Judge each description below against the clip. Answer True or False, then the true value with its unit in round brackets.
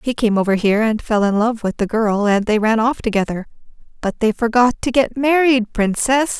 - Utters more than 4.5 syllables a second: True (5.2 syllables/s)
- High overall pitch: True (225 Hz)